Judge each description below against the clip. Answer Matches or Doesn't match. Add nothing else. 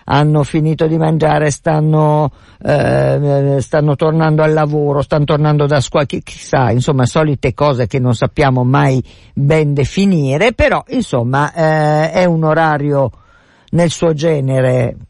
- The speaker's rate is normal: Matches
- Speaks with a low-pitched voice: Doesn't match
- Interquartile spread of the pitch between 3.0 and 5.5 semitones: Doesn't match